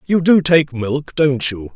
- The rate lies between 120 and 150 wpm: No, fast, 205 wpm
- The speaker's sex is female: No, male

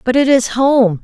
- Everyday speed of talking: No, fast, 235 wpm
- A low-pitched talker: No, high, 245 Hz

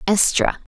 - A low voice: No, medium, 170 Hz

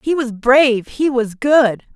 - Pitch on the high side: Yes, very high, 250 Hz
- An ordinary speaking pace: Yes, average, 185 wpm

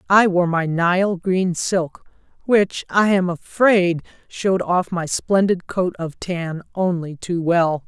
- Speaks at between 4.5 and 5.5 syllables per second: No, 3.5 syllables/s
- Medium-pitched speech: Yes, medium, 180 Hz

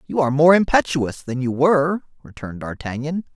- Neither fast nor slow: Yes, average, 160 wpm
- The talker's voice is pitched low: No, medium, 145 Hz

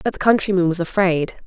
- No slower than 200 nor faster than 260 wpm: Yes, fast, 205 wpm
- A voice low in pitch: No, medium, 185 Hz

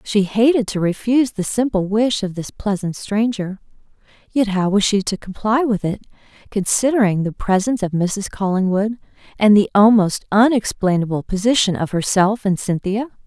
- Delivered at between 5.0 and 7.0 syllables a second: Yes, 5.1 syllables/s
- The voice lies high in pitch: Yes, high, 205 Hz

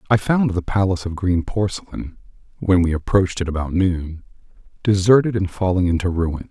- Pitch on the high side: No, very low, 95 Hz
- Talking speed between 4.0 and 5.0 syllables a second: No, 5.4 syllables/s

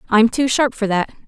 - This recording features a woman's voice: Yes, female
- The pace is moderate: No, fast, 235 wpm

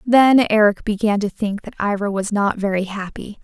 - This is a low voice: No, high, 210 Hz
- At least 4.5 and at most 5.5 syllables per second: Yes, 4.9 syllables/s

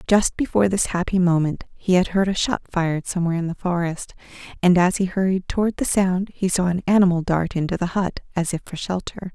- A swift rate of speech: Yes, fast, 220 wpm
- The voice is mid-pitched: Yes, medium, 180 Hz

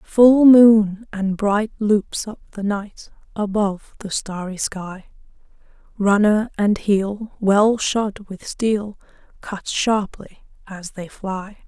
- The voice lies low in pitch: No, high, 205 Hz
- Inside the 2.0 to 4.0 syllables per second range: Yes, 3.1 syllables/s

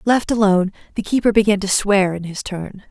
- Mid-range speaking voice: No, high, 200 Hz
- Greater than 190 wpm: Yes, fast, 205 wpm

